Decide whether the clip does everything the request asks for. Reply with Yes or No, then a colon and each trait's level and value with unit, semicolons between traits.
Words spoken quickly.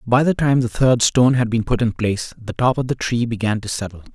Yes: fast, 275 wpm